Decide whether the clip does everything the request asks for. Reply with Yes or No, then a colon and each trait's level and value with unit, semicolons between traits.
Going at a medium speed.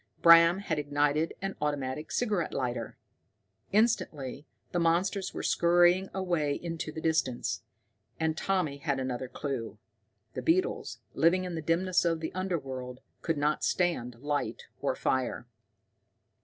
No: slow, 130 wpm